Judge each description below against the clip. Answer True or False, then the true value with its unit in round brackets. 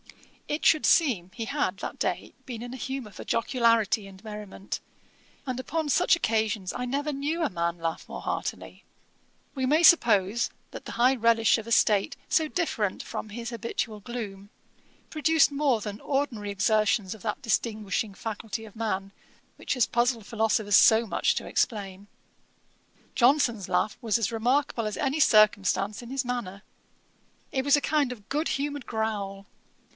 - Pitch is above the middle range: True (230 Hz)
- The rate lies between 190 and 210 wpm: False (160 wpm)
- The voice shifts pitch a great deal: False (4.3 semitones)